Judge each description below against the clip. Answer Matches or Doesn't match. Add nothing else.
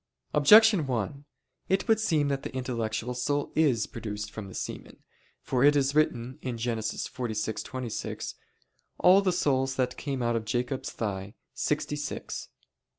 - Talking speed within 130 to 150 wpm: Matches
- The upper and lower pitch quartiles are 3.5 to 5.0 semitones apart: Matches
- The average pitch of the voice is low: Matches